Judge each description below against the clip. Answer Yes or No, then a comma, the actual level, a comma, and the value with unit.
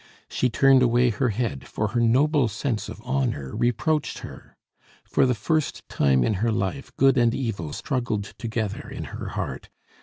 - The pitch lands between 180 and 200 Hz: No, low, 120 Hz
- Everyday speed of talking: Yes, average, 170 wpm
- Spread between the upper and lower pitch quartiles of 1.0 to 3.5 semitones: No, average, 3.9 semitones